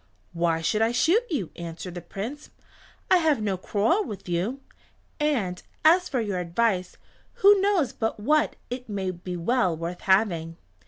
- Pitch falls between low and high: No, high, 210 Hz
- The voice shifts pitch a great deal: Yes, wide, 7.9 semitones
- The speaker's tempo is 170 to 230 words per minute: No, average, 160 wpm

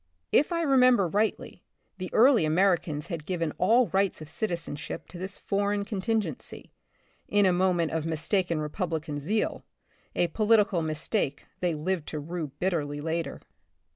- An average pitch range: Yes, average, 4.4 semitones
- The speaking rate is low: No, average, 145 wpm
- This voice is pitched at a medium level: Yes, medium, 180 Hz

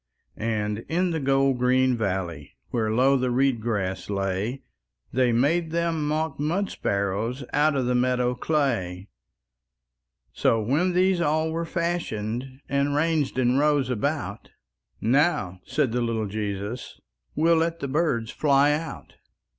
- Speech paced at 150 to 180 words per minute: No, average, 140 wpm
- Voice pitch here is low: Yes, low, 130 Hz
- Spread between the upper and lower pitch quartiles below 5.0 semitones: No, wide, 5.5 semitones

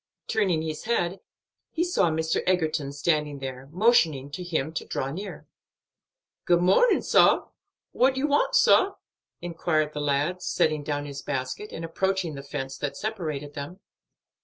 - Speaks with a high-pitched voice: No, medium, 160 Hz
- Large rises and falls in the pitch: No, average, 4.5 semitones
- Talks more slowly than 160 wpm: Yes, average, 150 wpm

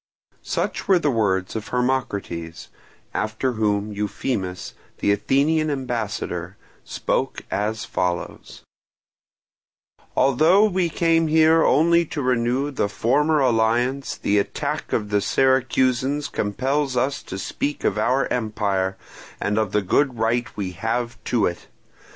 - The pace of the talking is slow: Yes, slow, 125 wpm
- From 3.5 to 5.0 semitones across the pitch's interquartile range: No, wide, 5.4 semitones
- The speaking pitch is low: Yes, low, 120 Hz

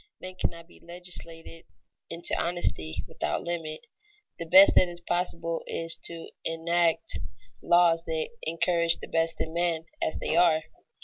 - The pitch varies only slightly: Yes, narrow, 1.0 semitones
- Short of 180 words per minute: Yes, average, 140 wpm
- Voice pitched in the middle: Yes, medium, 170 Hz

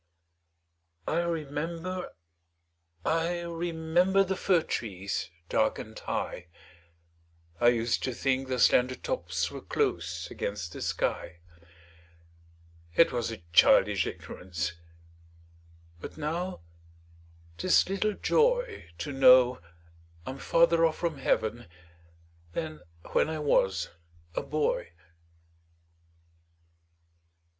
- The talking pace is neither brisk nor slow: No, slow, 100 wpm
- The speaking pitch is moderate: Yes, medium, 150 Hz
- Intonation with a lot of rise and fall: Yes, wide, 6.2 semitones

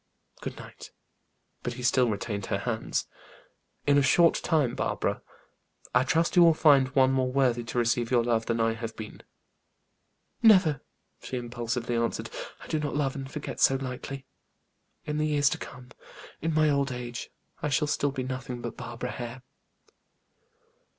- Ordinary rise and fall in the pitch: Yes, average, 3.1 semitones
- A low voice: Yes, low, 130 Hz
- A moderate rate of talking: Yes, average, 165 wpm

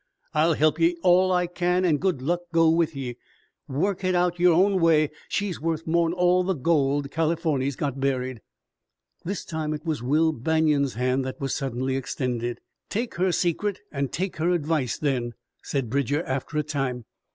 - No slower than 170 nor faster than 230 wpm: Yes, average, 175 wpm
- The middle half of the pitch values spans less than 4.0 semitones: No, average, 4.3 semitones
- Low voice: No, medium, 155 Hz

